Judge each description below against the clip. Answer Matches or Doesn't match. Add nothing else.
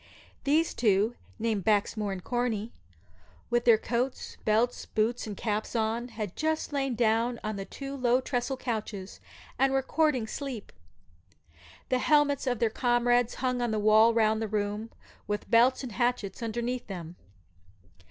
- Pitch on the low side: Doesn't match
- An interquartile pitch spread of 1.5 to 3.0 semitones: Matches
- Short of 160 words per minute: Matches